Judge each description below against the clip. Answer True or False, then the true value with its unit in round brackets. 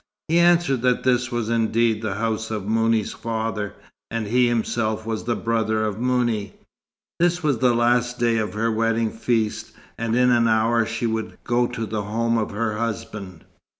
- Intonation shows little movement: True (1.6 semitones)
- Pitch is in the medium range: False (115 Hz)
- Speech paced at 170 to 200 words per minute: True (180 wpm)